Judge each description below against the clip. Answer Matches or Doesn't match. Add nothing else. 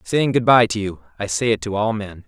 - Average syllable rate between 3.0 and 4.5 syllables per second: Doesn't match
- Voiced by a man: Matches